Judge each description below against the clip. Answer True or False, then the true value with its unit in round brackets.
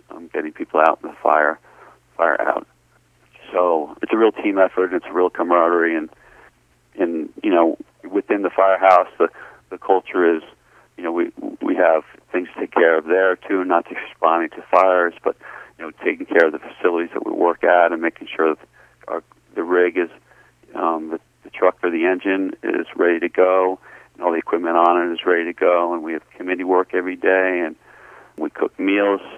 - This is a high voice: False (90 Hz)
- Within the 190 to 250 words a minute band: True (200 wpm)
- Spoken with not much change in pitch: True (1.8 semitones)